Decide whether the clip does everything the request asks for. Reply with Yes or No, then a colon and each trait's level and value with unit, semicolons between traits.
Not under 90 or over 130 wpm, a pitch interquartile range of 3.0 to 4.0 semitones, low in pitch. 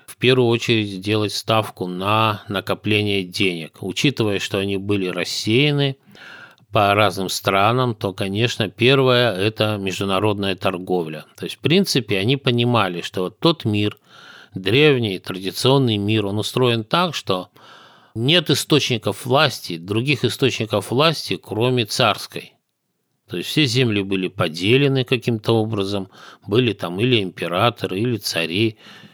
No: average, 125 wpm; average, 4.4 semitones; low, 110 Hz